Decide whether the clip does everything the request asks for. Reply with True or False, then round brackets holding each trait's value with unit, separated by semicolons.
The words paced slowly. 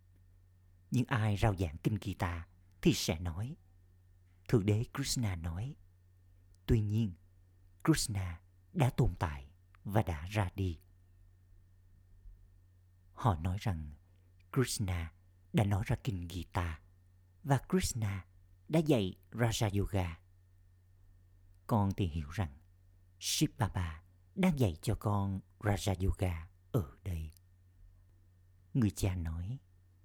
True (110 wpm)